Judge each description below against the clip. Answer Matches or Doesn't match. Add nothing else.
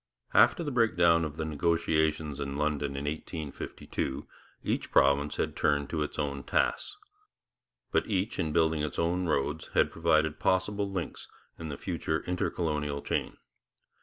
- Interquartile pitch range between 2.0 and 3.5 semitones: Matches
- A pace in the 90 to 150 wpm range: Matches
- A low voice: Matches